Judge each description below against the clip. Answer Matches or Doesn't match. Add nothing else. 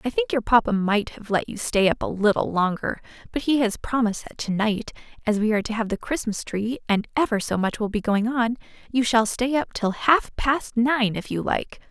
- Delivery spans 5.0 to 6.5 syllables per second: Matches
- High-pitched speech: Matches